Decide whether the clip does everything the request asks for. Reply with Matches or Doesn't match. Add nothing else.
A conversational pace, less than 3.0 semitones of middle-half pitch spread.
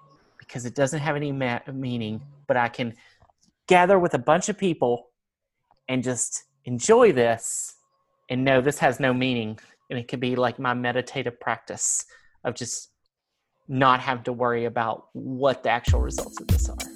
Matches